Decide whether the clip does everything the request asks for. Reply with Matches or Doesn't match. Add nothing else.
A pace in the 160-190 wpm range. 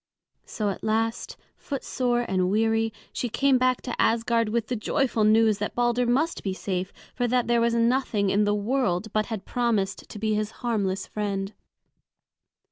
Matches